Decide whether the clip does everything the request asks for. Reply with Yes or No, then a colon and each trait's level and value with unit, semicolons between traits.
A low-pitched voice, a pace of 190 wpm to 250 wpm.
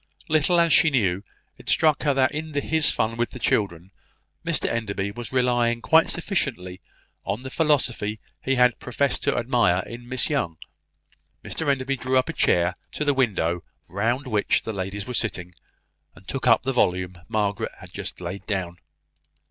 No: low, 120 Hz; average, 170 wpm